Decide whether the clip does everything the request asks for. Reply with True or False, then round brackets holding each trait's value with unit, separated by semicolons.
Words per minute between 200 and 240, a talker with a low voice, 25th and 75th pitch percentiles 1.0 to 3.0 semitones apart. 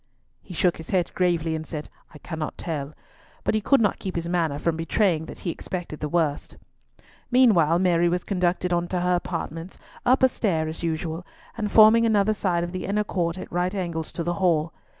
False (205 wpm; 175 Hz; 2.6 semitones)